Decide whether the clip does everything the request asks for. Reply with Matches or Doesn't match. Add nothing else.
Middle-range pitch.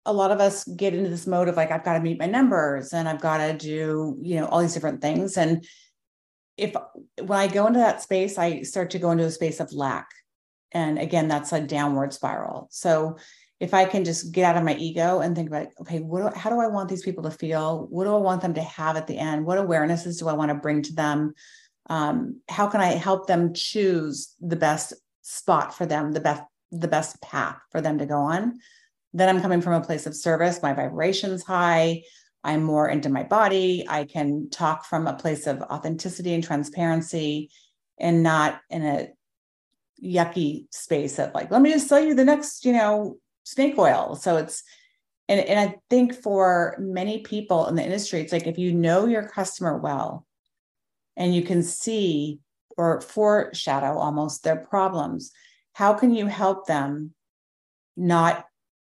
Matches